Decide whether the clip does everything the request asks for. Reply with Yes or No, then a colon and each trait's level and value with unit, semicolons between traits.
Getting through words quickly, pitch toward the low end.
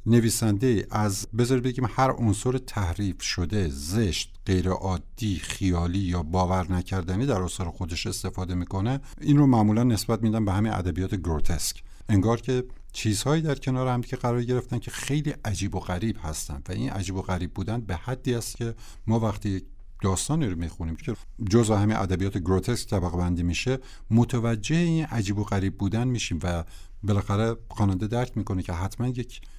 Yes: fast, 165 wpm; low, 105 Hz